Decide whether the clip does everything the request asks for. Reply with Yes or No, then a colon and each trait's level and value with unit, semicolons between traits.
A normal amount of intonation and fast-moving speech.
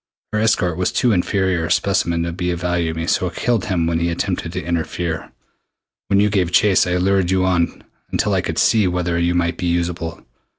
No: narrow, 1.8 semitones; fast, 220 wpm